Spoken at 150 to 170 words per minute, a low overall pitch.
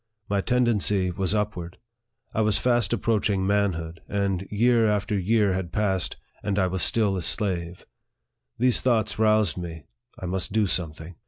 Yes: average, 155 wpm; low, 100 Hz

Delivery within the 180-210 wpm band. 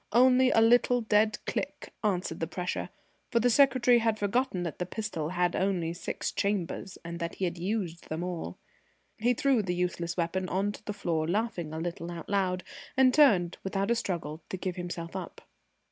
Yes: average, 190 wpm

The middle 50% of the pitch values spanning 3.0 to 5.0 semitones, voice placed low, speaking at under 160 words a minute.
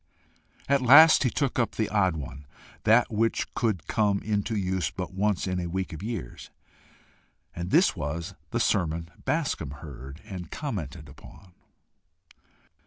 No: wide, 5.4 semitones; very low, 95 Hz; average, 145 wpm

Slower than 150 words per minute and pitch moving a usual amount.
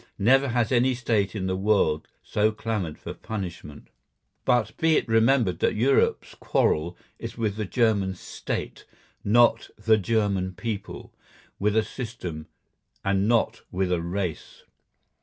Yes: average, 140 wpm; average, 3.6 semitones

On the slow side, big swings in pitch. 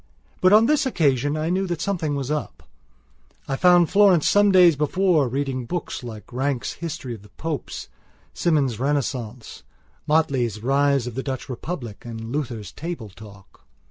No: average, 155 wpm; wide, 6.0 semitones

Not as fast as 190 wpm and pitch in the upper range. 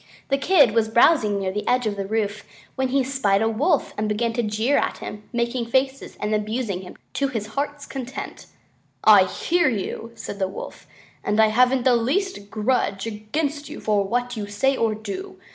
No: average, 195 wpm; high, 230 Hz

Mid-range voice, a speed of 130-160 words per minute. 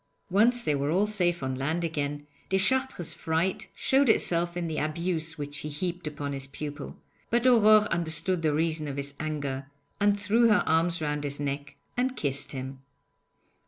No: medium, 160 Hz; average, 170 wpm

